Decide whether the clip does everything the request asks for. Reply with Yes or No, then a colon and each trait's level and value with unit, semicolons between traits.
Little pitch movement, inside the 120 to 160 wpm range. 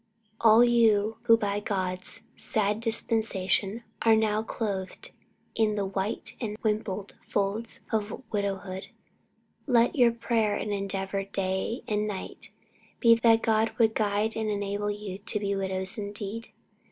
Yes: narrow, 2.1 semitones; average, 140 wpm